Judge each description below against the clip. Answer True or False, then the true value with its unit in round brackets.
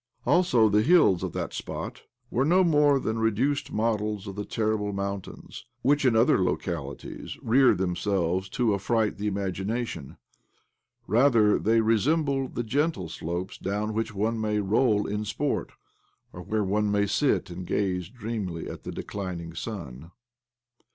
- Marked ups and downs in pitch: False (3.4 semitones)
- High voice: False (105 Hz)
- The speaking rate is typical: True (145 wpm)